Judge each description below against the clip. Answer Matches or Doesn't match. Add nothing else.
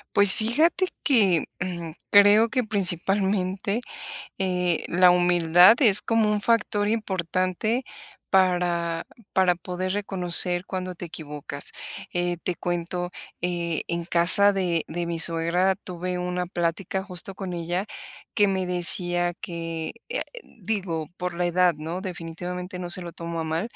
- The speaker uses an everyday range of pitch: Doesn't match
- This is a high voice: Doesn't match